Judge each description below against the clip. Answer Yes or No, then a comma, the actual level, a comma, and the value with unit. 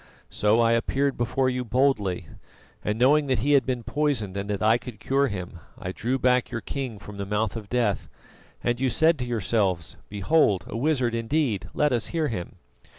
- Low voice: Yes, low, 120 Hz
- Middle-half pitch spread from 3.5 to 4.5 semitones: Yes, average, 4.2 semitones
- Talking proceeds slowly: No, average, 195 wpm